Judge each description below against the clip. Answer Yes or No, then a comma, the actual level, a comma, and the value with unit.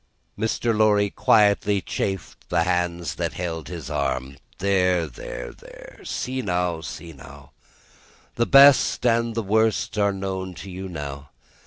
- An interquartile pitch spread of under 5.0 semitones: Yes, average, 4.3 semitones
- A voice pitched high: No, very low, 95 Hz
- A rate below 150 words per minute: Yes, average, 140 wpm